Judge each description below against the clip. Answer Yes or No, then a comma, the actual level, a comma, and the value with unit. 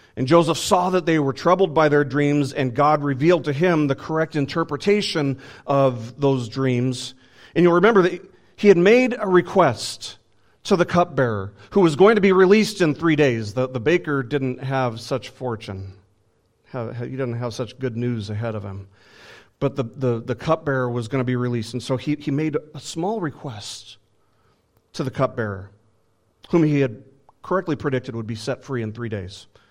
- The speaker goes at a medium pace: Yes, average, 185 wpm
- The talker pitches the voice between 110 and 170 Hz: Yes, low, 135 Hz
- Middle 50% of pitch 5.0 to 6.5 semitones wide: Yes, wide, 5.4 semitones